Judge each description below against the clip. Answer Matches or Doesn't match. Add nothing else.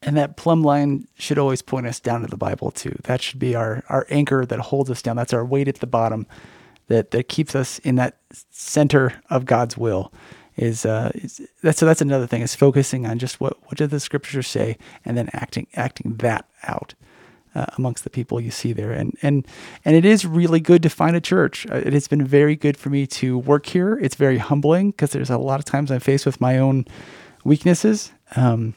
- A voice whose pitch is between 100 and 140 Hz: Matches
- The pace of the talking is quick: Matches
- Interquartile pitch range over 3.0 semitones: Matches